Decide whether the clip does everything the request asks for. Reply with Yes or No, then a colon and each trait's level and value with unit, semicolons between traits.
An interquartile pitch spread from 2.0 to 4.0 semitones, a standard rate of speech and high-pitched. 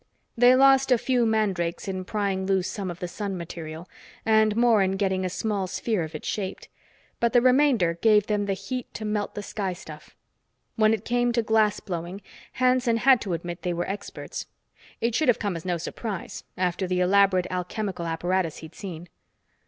Yes: average, 3.7 semitones; average, 190 wpm; high, 200 Hz